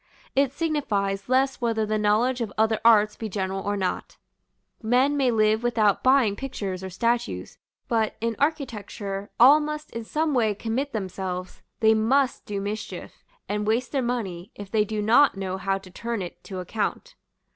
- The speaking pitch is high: Yes, high, 220 Hz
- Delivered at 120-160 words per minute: No, average, 170 wpm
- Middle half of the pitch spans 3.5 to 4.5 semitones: Yes, average, 3.9 semitones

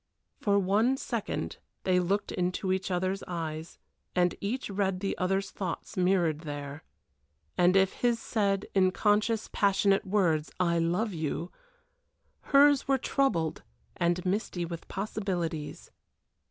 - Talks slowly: Yes, slow, 125 wpm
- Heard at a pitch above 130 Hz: Yes, high, 190 Hz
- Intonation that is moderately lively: Yes, average, 3.0 semitones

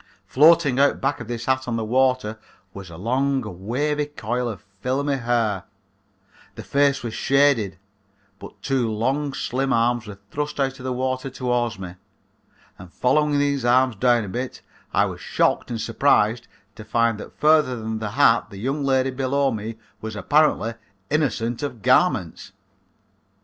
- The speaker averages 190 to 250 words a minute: No, average, 160 wpm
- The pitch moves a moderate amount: Yes, average, 3.6 semitones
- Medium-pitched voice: No, low, 125 Hz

